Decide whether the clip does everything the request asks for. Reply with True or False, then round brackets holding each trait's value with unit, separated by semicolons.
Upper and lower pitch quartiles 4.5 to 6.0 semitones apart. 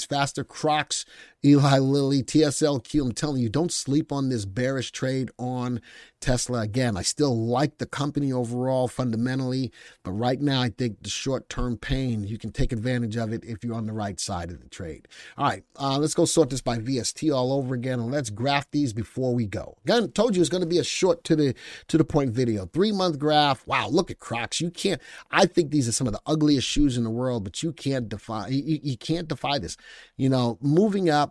False (3.8 semitones)